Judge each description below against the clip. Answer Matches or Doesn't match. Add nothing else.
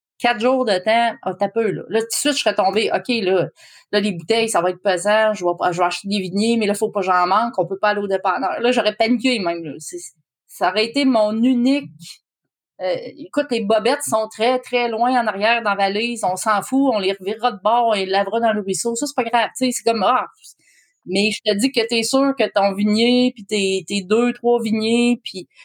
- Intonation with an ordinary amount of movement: Matches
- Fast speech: Matches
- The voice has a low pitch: Doesn't match